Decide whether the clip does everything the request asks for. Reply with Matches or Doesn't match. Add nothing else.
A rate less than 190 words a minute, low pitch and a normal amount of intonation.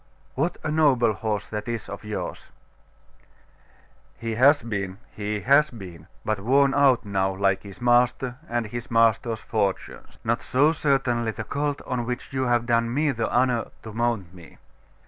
Matches